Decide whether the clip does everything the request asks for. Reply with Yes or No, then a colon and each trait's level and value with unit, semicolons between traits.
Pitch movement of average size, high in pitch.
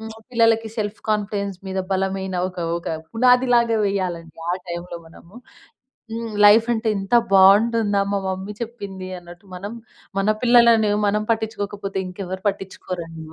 Yes: average, 3.1 semitones; high, 200 Hz